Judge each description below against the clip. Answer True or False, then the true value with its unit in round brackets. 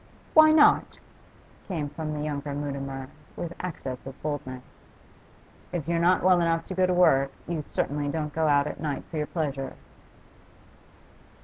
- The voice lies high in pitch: False (150 Hz)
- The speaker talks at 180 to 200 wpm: False (155 wpm)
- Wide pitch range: False (3.3 semitones)